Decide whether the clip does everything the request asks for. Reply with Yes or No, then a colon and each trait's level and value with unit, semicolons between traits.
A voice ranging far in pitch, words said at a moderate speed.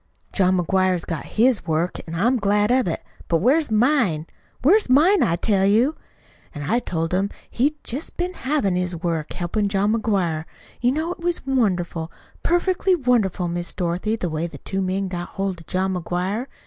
Yes: wide, 6.3 semitones; average, 180 wpm